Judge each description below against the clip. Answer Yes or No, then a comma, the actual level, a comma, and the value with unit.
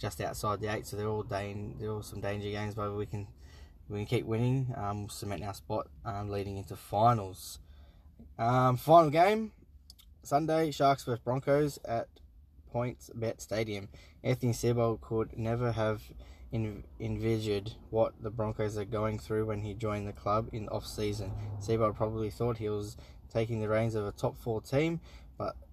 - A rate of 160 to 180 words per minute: Yes, average, 175 wpm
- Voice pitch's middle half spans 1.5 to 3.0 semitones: Yes, narrow, 2.4 semitones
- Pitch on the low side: Yes, low, 110 Hz